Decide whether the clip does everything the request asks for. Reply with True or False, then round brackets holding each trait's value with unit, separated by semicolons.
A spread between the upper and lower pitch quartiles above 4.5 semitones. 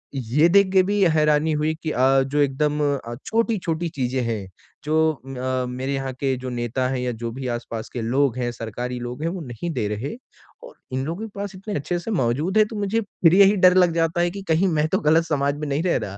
True (5.5 semitones)